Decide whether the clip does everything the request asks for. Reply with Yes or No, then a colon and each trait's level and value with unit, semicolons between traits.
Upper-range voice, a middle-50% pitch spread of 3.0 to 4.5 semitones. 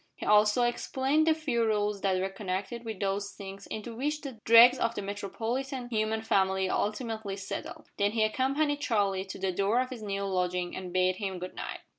Yes: high, 210 Hz; average, 3.7 semitones